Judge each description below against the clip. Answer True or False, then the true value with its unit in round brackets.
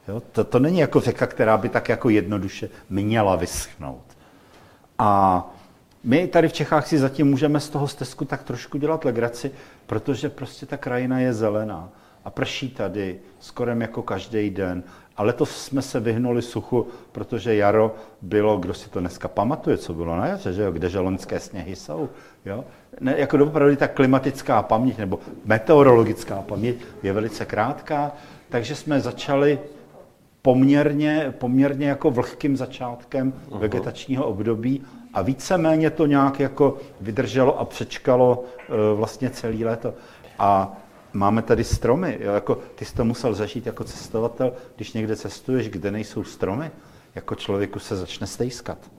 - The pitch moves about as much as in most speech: True (4.6 semitones)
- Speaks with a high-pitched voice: False (120 Hz)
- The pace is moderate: True (150 wpm)